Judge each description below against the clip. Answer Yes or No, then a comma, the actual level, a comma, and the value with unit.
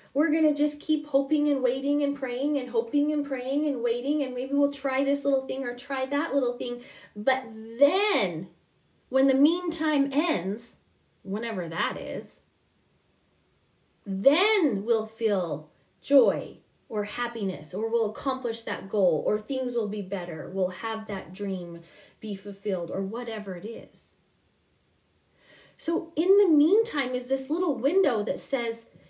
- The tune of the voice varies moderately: Yes, average, 4.8 semitones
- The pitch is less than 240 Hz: No, very high, 260 Hz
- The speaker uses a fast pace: No, average, 150 wpm